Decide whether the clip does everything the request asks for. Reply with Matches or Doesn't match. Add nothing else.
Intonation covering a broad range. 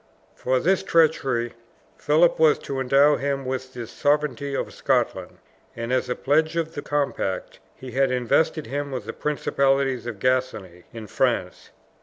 Doesn't match